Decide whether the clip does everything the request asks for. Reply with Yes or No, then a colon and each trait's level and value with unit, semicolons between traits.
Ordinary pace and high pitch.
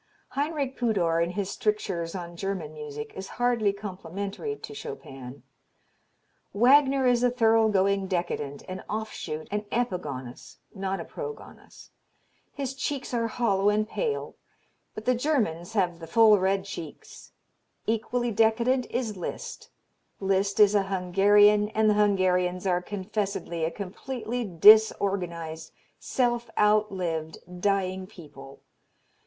No: slow, 125 wpm; high, 200 Hz